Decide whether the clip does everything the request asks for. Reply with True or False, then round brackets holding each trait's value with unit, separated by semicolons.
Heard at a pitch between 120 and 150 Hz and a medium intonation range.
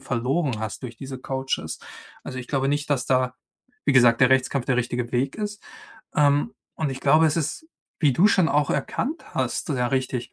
True (135 Hz; 3.0 semitones)